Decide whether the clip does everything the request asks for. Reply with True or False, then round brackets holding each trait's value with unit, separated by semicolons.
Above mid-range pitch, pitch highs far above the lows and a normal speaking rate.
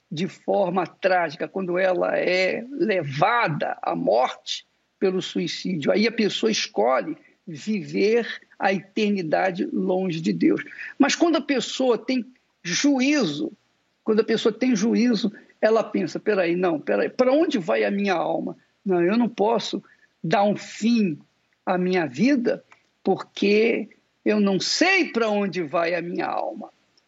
False (210 Hz; 4.9 semitones; 140 wpm)